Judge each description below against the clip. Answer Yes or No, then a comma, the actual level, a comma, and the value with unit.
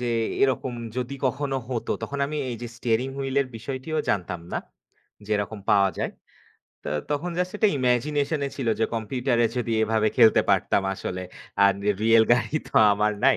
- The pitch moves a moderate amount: Yes, average, 3.7 semitones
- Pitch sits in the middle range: No, low, 120 Hz